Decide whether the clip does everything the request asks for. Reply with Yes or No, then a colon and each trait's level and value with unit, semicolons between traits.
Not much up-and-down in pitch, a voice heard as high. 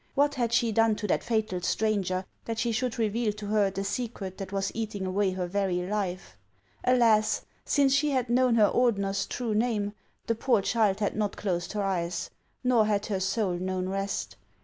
No: average, 3.1 semitones; high, 210 Hz